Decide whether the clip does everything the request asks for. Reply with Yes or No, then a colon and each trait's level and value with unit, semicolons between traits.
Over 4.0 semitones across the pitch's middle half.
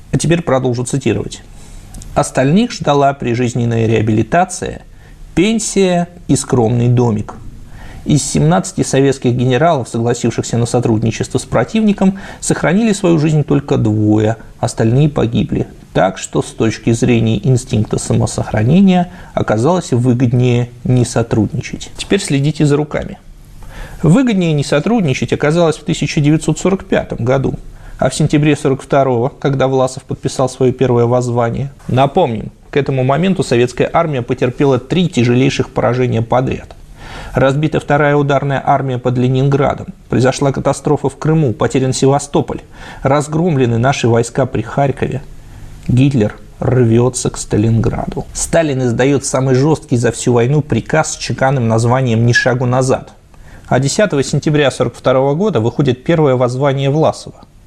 No: average, 3.6 semitones